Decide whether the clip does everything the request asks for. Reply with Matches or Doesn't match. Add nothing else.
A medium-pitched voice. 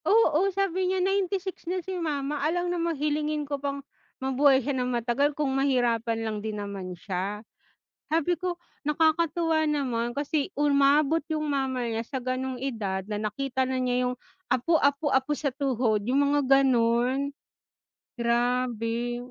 Doesn't match